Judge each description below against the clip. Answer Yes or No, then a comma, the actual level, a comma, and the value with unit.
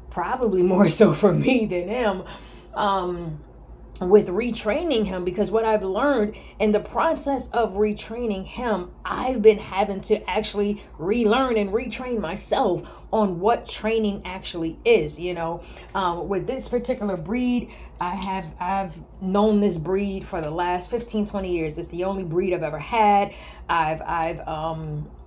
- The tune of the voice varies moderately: Yes, average, 3.6 semitones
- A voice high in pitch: Yes, high, 200 Hz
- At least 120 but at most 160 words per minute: Yes, average, 150 wpm